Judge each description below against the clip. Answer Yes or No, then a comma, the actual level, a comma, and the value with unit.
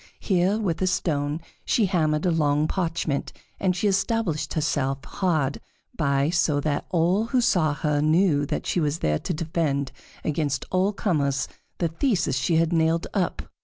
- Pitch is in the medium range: Yes, medium, 160 Hz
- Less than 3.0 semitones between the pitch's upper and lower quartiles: No, average, 3.9 semitones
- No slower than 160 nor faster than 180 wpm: Yes, average, 165 wpm